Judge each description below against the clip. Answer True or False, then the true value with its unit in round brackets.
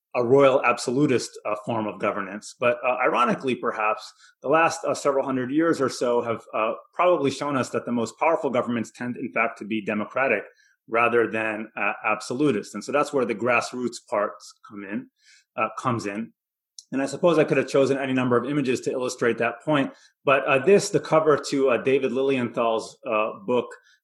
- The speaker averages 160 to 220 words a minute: True (190 wpm)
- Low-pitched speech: True (125 Hz)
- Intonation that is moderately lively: True (3.2 semitones)